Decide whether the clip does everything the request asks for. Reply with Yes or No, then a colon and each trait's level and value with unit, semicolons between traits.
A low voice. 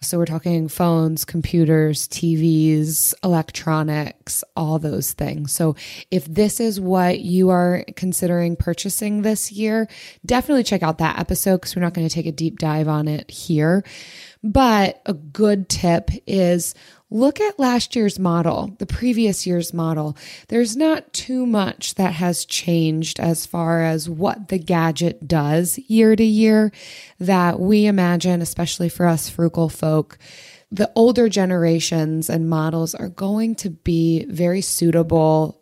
No: medium, 175 Hz